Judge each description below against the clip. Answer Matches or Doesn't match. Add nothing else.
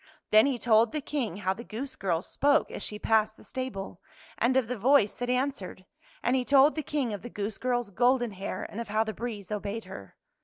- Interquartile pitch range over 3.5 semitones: Matches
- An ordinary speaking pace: Doesn't match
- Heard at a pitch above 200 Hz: Matches